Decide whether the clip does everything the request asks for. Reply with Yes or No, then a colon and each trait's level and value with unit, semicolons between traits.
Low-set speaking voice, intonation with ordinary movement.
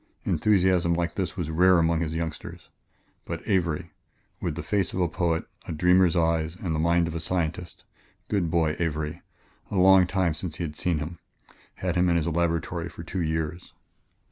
No: very low, 85 Hz; narrow, 1.9 semitones